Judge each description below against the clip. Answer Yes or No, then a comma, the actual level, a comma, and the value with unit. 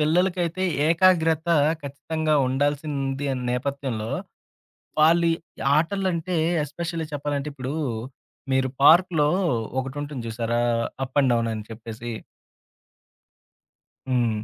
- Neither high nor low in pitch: Yes, medium, 145 Hz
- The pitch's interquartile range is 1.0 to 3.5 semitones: No, average, 4.2 semitones